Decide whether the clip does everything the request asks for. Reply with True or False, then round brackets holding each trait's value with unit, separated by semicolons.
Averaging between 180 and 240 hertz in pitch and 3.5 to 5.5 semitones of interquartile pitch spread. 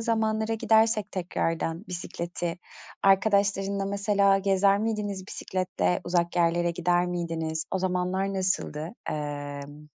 False (185 Hz; 2.8 semitones)